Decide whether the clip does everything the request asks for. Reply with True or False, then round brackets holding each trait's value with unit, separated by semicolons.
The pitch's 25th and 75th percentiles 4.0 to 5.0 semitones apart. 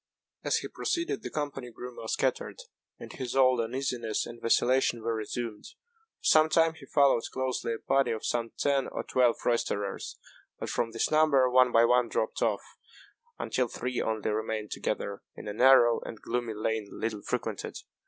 False (2.8 semitones)